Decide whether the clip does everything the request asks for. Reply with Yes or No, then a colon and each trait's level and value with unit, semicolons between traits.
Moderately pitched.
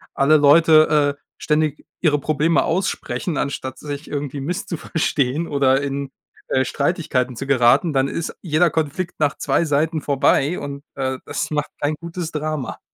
Yes: medium, 150 Hz